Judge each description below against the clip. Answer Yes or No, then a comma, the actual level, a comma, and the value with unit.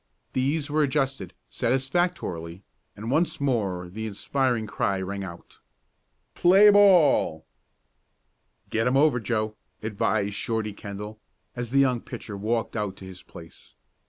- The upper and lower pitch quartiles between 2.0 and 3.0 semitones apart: No, wide, 5.5 semitones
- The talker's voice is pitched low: Yes, low, 115 Hz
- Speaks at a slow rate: Yes, slow, 130 wpm